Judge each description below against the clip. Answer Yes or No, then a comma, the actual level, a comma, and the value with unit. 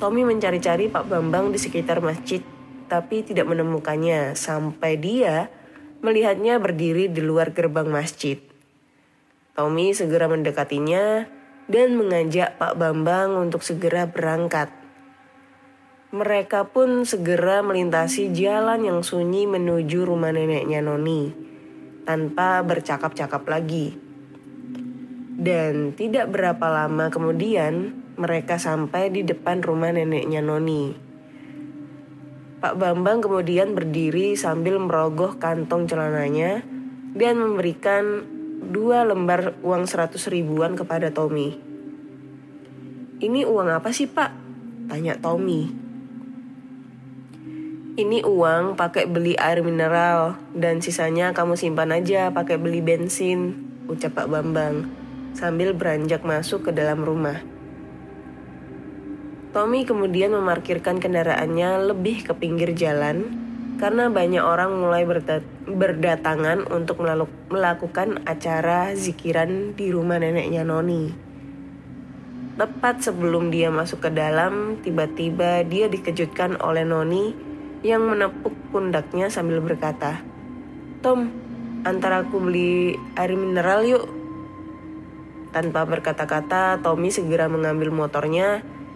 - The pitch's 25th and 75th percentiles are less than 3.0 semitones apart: No, average, 4.6 semitones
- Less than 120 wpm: Yes, average, 105 wpm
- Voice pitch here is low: No, medium, 175 Hz